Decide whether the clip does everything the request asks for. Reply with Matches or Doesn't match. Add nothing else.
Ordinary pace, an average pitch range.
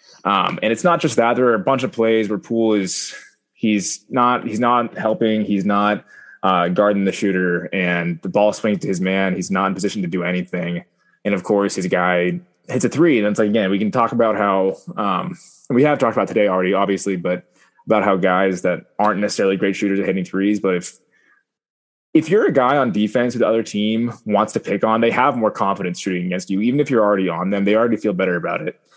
Doesn't match